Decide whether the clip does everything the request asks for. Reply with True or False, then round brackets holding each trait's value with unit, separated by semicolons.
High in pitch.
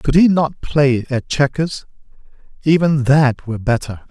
False (140 Hz)